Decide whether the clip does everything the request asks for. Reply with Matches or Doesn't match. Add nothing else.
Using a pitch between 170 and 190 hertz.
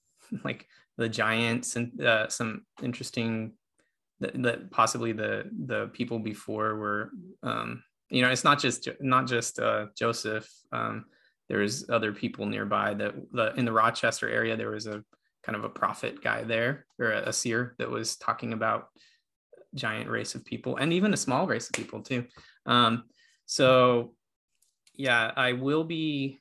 Doesn't match